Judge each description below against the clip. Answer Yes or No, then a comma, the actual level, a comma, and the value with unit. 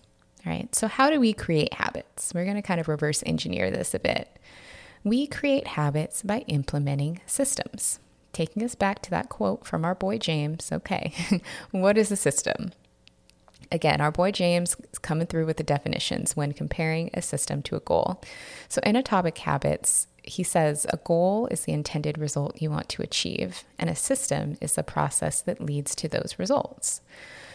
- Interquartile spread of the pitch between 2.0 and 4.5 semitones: No, average, 5.1 semitones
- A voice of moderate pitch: Yes, medium, 165 Hz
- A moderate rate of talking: Yes, average, 180 wpm